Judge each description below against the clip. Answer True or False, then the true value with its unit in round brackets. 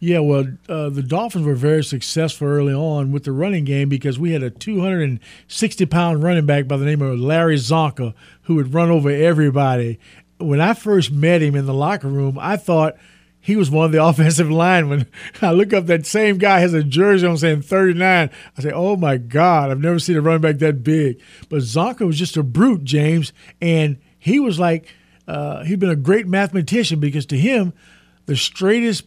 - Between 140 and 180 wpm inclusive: False (200 wpm)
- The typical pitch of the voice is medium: True (160 Hz)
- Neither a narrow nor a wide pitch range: True (3.9 semitones)